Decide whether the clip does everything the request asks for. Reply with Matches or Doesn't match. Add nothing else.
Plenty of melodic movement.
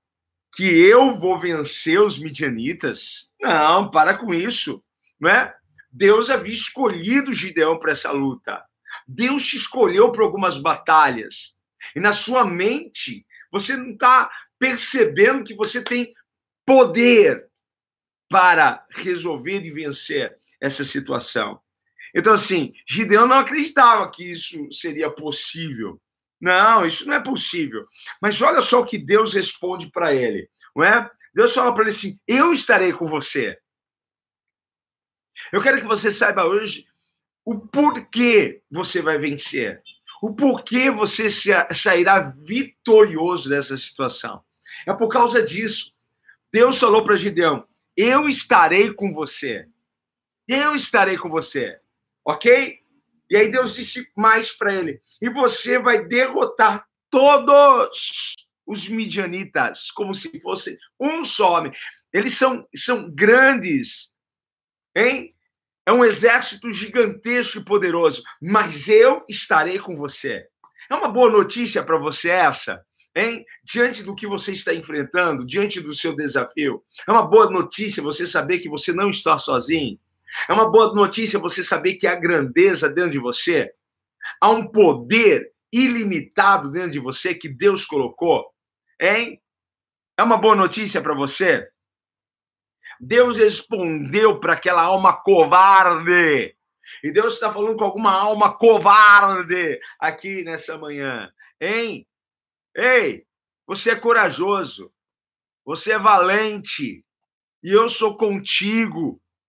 Matches